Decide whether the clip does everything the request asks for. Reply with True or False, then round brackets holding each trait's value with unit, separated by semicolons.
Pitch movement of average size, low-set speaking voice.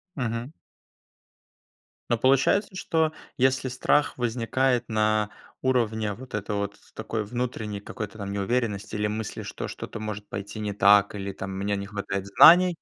True (3.6 semitones; 110 Hz)